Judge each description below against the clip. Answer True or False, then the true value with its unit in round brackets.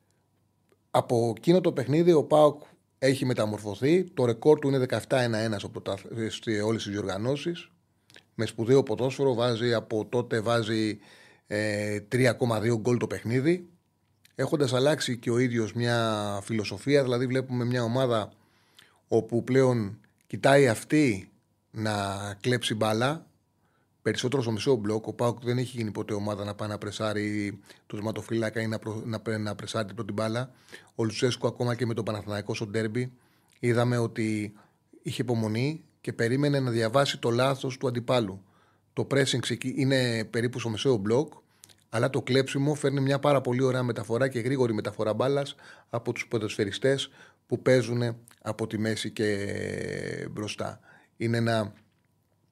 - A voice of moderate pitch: False (115 Hz)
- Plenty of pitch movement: False (3.1 semitones)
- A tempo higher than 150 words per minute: False (145 wpm)